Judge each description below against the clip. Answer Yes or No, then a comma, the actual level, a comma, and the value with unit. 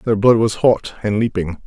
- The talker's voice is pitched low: Yes, low, 110 Hz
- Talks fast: Yes, fast, 215 wpm